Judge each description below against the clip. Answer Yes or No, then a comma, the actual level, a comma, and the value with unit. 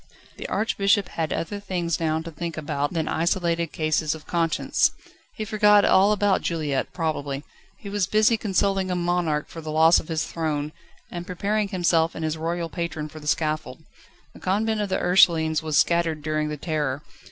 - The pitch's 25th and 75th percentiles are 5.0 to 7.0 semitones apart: No, average, 3.4 semitones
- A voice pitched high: No, medium, 165 Hz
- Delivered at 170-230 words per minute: Yes, average, 180 wpm